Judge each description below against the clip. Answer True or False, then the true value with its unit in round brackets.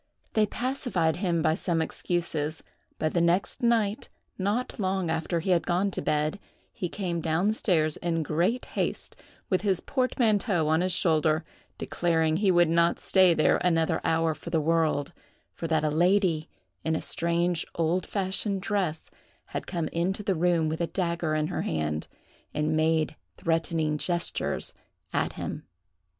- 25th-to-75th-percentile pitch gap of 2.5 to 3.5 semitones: True (2.9 semitones)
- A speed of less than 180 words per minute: True (160 wpm)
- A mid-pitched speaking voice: True (170 Hz)